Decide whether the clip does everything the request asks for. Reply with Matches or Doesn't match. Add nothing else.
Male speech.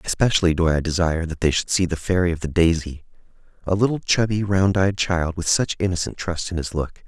Matches